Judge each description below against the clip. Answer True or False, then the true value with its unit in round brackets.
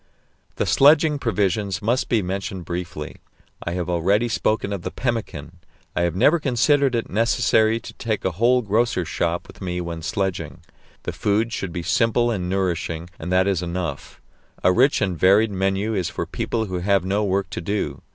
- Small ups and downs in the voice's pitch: False (4.2 semitones)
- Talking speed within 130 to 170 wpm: False (180 wpm)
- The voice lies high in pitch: False (100 Hz)